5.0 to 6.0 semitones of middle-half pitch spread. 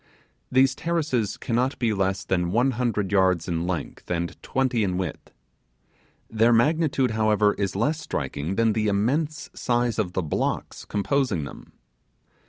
Yes: average, 5.3 semitones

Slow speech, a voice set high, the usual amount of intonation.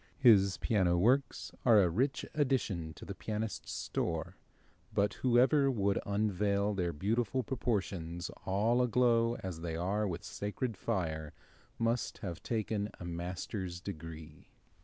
No: slow, 130 wpm; low, 100 Hz; average, 4.9 semitones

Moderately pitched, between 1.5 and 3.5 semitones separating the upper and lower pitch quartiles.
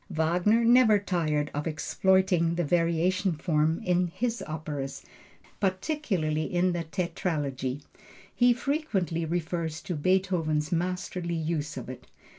Yes: medium, 170 Hz; average, 3.2 semitones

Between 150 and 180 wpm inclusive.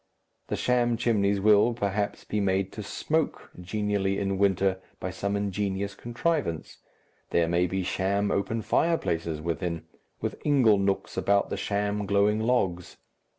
No: average, 140 wpm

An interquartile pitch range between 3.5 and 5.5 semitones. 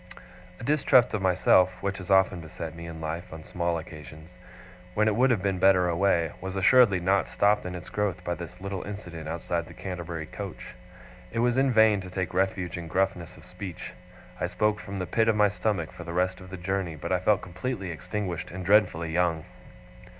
No: average, 2.7 semitones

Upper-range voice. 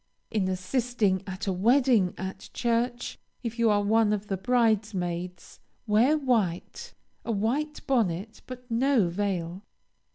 Yes: high, 215 Hz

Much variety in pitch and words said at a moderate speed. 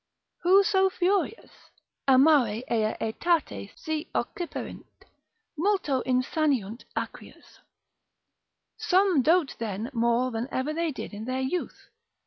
No: wide, 6.8 semitones; slow, 110 wpm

